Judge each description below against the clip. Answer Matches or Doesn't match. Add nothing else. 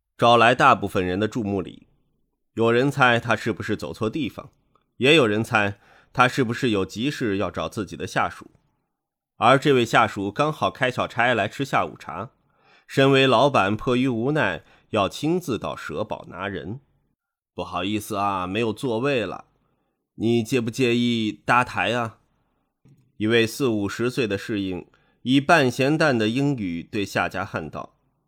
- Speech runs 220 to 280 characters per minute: Matches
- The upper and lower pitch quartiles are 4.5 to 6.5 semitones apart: Doesn't match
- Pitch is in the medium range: Doesn't match